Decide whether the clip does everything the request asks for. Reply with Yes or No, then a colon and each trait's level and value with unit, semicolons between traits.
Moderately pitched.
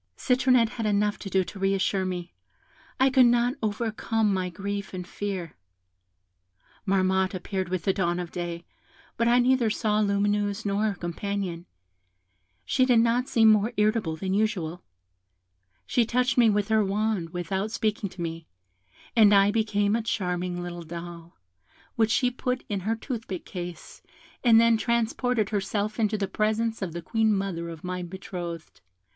No: high, 205 Hz